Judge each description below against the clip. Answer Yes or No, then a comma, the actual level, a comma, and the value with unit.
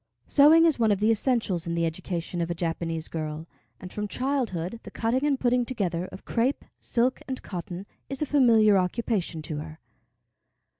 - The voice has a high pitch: Yes, high, 205 Hz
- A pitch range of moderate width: No, wide, 6.7 semitones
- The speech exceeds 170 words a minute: Yes, average, 180 wpm